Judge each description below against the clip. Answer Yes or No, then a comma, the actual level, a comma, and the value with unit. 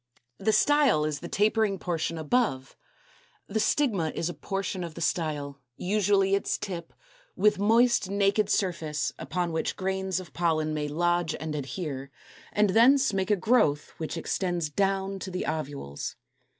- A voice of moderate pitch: Yes, medium, 180 Hz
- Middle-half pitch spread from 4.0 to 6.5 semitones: Yes, average, 4.4 semitones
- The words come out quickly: No, average, 150 wpm